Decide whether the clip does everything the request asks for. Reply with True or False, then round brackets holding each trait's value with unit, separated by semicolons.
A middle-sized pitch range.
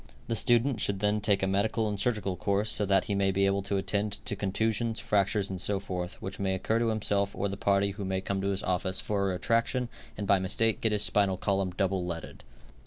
False (1.7 semitones)